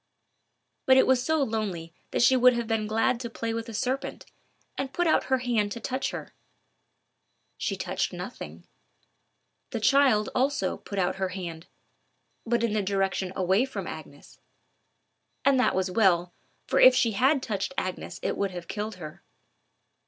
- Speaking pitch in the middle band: No, high, 225 Hz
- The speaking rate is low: No, average, 165 wpm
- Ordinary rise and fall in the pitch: Yes, average, 5.0 semitones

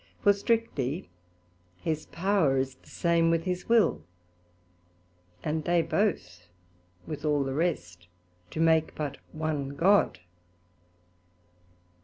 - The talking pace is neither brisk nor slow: No, slow, 110 wpm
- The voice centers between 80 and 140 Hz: No, medium, 160 Hz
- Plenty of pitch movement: No, average, 4.2 semitones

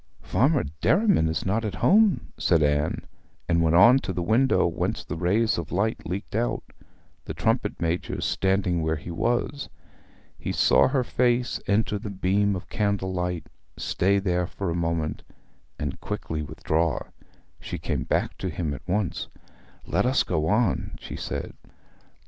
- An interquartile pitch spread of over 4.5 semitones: Yes, average, 4.9 semitones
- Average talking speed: Yes, average, 155 wpm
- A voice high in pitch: No, very low, 95 Hz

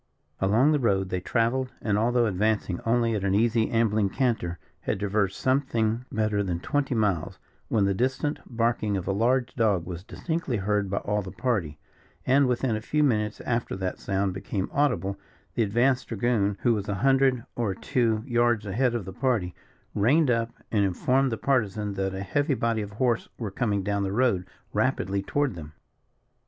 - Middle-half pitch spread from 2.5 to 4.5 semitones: Yes, average, 3.9 semitones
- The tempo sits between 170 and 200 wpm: Yes, average, 180 wpm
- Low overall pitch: Yes, low, 110 Hz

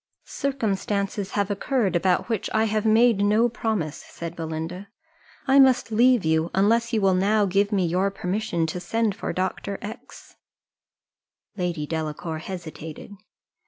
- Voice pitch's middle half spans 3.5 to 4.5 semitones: Yes, average, 4.2 semitones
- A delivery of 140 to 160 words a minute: Yes, average, 145 wpm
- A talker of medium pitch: No, high, 200 Hz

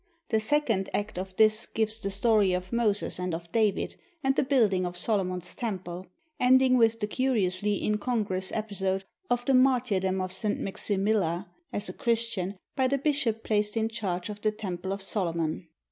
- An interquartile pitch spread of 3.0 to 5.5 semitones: Yes, average, 3.5 semitones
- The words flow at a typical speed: Yes, average, 170 wpm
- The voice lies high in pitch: Yes, high, 210 Hz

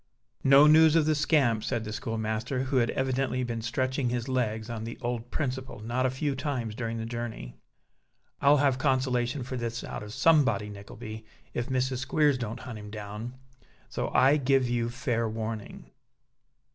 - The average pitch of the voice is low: Yes, low, 125 Hz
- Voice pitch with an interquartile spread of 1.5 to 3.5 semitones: Yes, average, 2.8 semitones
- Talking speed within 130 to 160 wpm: No, average, 170 wpm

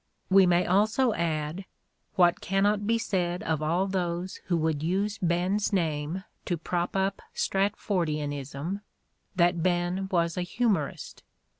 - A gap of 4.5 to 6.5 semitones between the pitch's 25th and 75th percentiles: No, narrow, 2.6 semitones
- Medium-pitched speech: Yes, medium, 180 Hz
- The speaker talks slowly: Yes, slow, 130 wpm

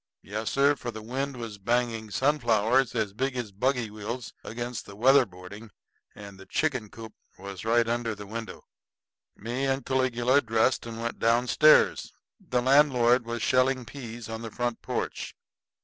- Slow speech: No, average, 160 wpm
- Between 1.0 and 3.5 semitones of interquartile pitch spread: Yes, average, 2.7 semitones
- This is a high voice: No, low, 120 Hz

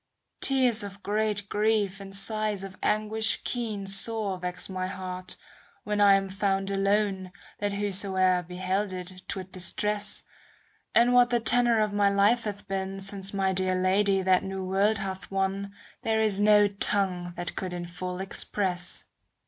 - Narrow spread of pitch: Yes, narrow, 1.9 semitones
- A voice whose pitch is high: Yes, high, 195 Hz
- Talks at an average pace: Yes, average, 160 wpm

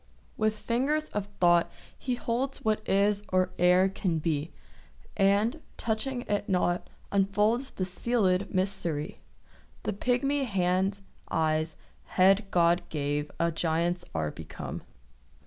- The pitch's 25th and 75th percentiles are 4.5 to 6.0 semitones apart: No, average, 3.9 semitones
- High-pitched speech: Yes, high, 195 Hz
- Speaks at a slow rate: Yes, slow, 120 wpm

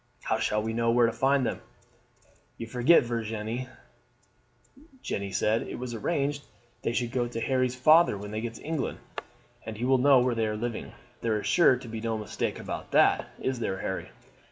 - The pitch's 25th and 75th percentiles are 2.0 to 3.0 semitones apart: Yes, narrow, 2.6 semitones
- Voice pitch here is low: Yes, low, 120 Hz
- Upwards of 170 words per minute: Yes, average, 195 wpm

